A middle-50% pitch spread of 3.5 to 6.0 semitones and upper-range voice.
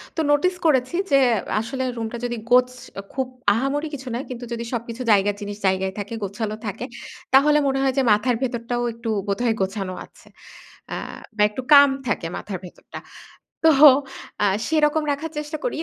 Yes: average, 4.7 semitones; high, 245 Hz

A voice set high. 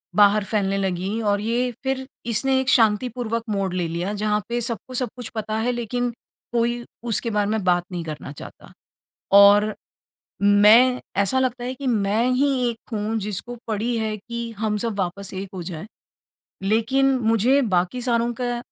Yes: high, 220 Hz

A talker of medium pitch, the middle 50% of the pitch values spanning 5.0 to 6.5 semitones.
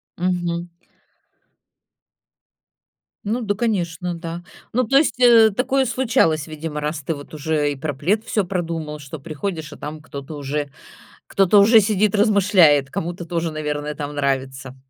Yes: medium, 165 Hz; average, 5.3 semitones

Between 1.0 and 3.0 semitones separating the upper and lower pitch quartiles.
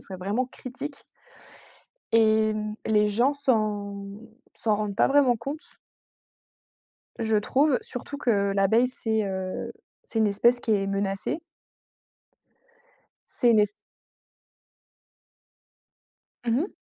No: average, 3.6 semitones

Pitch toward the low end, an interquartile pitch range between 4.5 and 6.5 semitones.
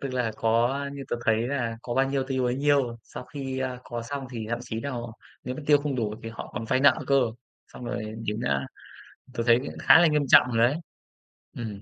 No: low, 125 Hz; average, 3.1 semitones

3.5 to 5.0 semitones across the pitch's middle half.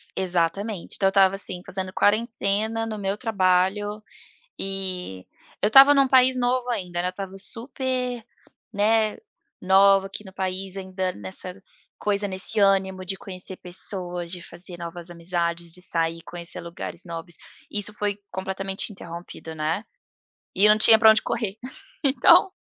No: average, 2.8 semitones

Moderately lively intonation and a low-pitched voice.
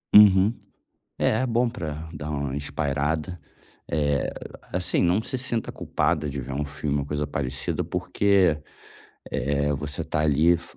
Yes: average, 4.1 semitones; very low, 75 Hz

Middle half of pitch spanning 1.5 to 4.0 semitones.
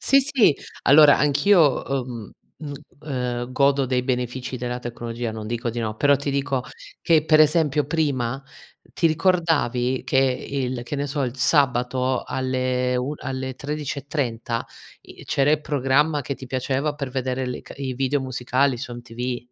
Yes: narrow, 2.6 semitones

